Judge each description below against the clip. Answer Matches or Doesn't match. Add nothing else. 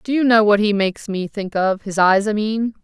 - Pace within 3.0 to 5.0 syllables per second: Doesn't match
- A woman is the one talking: Matches